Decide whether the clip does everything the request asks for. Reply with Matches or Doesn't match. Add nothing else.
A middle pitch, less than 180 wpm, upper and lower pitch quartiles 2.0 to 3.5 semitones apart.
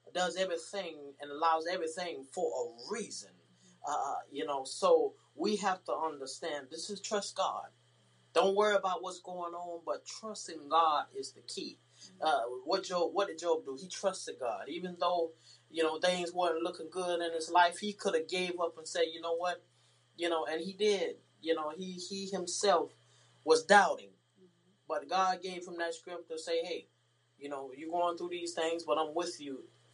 Doesn't match